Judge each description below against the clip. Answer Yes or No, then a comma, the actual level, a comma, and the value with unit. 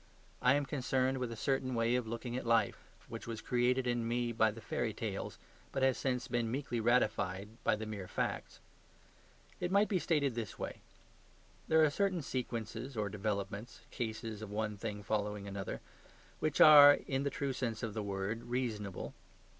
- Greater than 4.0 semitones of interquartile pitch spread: No, average, 3.5 semitones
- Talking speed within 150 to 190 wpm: Yes, average, 180 wpm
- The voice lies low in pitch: Yes, low, 120 Hz